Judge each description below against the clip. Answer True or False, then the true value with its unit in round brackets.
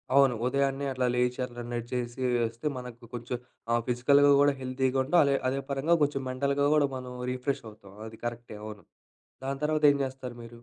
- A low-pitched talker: True (130 Hz)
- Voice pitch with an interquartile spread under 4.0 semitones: True (2.6 semitones)